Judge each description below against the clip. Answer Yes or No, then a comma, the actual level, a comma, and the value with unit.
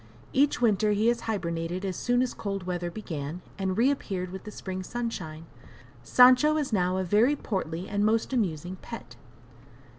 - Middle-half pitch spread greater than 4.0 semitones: Yes, average, 4.7 semitones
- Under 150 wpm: No, average, 160 wpm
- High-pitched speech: Yes, high, 200 Hz